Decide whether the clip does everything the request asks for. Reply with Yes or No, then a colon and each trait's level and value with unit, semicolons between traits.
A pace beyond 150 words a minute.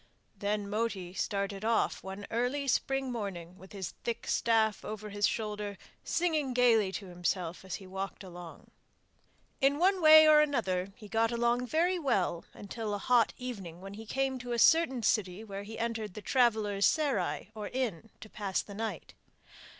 Yes: average, 170 wpm